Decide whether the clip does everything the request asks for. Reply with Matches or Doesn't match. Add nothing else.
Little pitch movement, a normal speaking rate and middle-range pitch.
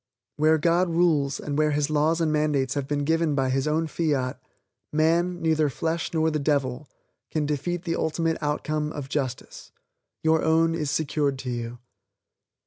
Matches